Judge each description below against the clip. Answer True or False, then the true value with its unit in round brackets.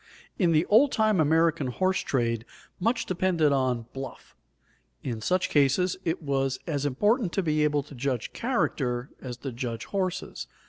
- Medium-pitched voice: True (150 Hz)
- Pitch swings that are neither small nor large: False (5.8 semitones)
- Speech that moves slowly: False (155 wpm)